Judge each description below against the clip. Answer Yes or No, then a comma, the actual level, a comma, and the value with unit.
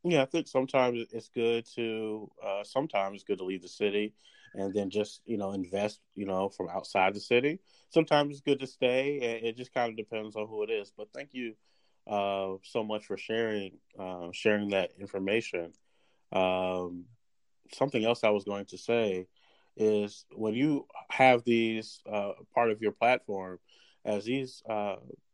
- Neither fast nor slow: Yes, average, 180 wpm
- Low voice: Yes, low, 105 Hz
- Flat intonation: No, average, 3.4 semitones